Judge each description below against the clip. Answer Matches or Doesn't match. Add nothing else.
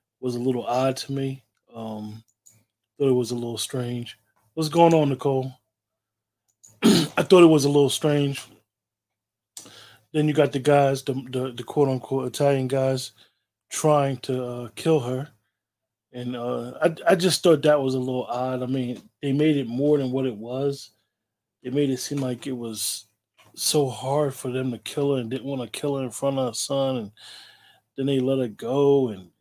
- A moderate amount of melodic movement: Matches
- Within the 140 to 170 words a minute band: Doesn't match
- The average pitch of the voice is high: Doesn't match